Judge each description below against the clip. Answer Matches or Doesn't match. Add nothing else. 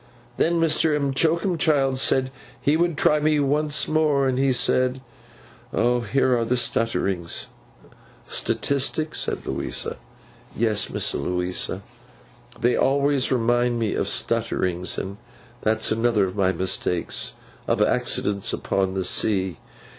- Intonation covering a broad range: Matches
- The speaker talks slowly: Matches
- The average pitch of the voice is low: Matches